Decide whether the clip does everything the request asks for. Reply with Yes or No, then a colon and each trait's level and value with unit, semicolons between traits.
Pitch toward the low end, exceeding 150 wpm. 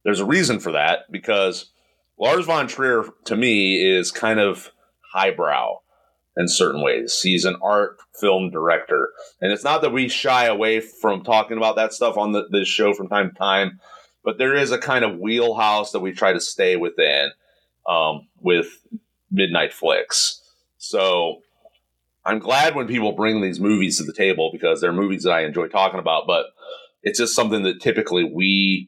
Yes: low, 105 Hz; average, 180 wpm